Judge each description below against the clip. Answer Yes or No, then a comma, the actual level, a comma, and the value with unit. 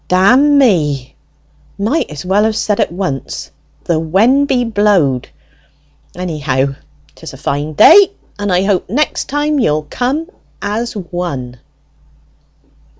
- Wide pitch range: Yes, wide, 8.1 semitones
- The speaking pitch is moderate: No, high, 195 Hz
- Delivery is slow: Yes, slow, 120 wpm